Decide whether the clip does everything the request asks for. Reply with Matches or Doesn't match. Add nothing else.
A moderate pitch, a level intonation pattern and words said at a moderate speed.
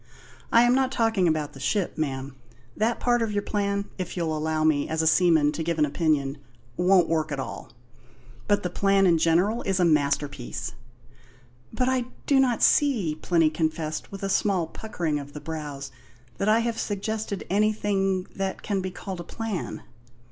Doesn't match